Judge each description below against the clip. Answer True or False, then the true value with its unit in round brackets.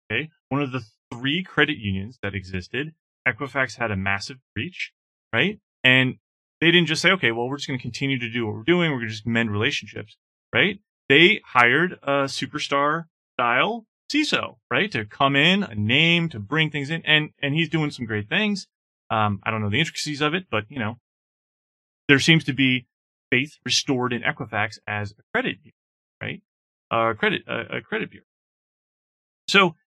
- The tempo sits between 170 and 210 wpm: True (185 wpm)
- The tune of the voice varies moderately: False (5.7 semitones)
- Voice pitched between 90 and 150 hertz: True (135 Hz)